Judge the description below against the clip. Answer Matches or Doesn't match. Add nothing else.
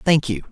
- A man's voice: Matches